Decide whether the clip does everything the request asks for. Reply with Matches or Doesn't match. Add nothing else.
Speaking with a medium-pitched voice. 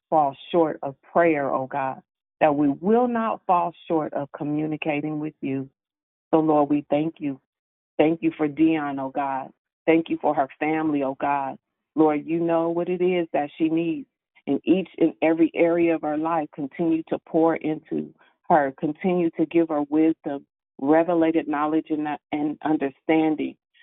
Matches